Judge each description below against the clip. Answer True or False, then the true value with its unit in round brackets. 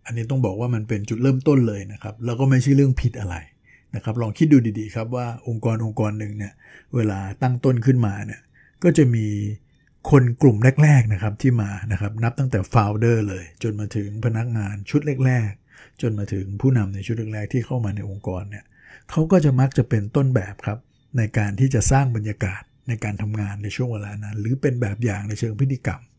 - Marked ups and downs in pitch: False (3.7 semitones)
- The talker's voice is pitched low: True (115 Hz)